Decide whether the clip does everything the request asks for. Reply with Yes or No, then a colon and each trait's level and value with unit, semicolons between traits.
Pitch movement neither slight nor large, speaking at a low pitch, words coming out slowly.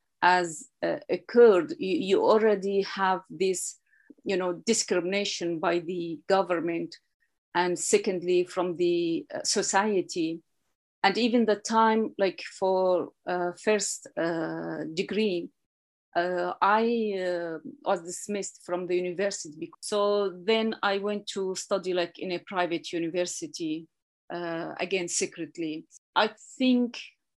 No: average, 3.2 semitones; high, 190 Hz; slow, 115 wpm